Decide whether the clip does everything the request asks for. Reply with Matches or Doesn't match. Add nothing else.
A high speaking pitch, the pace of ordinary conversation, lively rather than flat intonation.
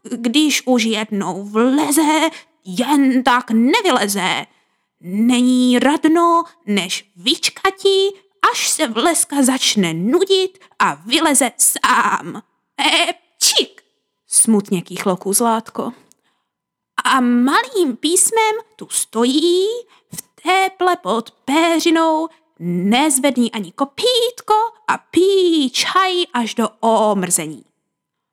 Doesn't match